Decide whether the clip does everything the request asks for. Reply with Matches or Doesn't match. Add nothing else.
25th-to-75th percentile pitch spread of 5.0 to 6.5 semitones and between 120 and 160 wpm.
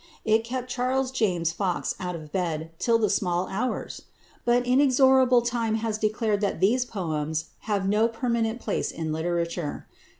Matches